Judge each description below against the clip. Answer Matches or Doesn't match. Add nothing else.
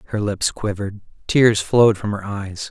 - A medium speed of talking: Matches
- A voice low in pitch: Matches